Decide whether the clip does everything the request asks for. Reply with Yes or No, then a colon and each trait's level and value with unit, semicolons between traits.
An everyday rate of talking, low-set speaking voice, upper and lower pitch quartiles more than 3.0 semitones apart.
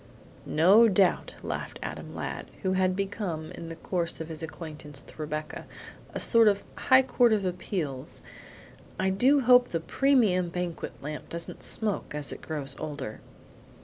No: average, 150 wpm; medium, 175 Hz; average, 4.5 semitones